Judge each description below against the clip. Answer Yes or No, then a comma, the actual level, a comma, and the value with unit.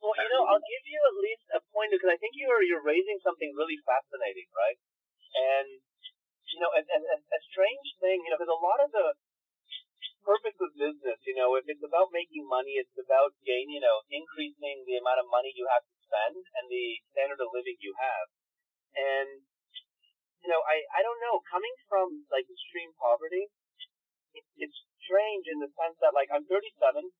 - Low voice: No, high, 215 Hz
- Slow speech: No, average, 195 wpm